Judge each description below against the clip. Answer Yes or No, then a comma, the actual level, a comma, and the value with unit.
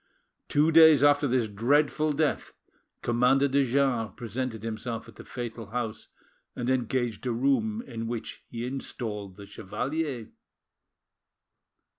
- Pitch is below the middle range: Yes, low, 125 Hz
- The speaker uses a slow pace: Yes, slow, 125 wpm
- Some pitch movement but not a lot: Yes, average, 3.6 semitones